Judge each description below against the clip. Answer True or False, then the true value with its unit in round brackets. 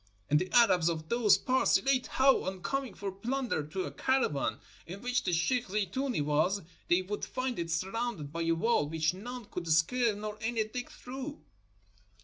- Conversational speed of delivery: True (180 wpm)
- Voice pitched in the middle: False (205 Hz)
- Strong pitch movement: True (6.6 semitones)